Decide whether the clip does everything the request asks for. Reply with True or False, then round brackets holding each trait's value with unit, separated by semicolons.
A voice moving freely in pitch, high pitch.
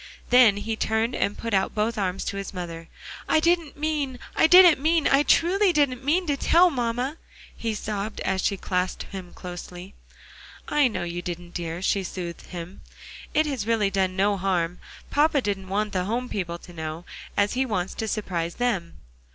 True (6.6 semitones; 205 Hz)